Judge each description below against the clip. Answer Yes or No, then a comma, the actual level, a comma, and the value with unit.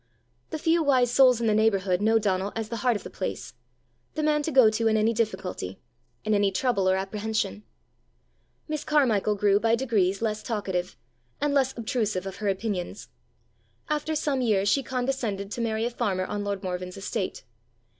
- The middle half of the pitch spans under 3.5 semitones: No, average, 3.9 semitones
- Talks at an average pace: Yes, average, 180 wpm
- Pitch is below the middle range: No, high, 220 Hz